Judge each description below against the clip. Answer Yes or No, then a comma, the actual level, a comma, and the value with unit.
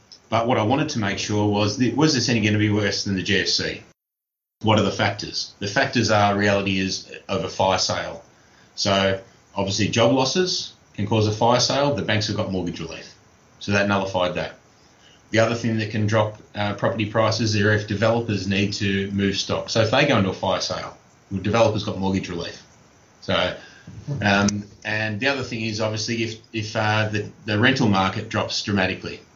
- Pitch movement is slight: Yes, narrow, 2.3 semitones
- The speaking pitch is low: Yes, low, 105 Hz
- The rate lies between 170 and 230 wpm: Yes, average, 190 wpm